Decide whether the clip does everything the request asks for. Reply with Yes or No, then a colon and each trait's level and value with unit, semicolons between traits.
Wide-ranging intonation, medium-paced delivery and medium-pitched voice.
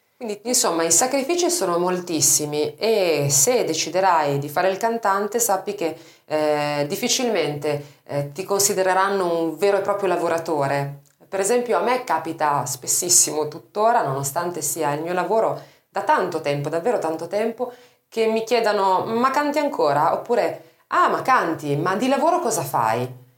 Yes: wide, 6.6 semitones; average, 150 wpm; medium, 180 Hz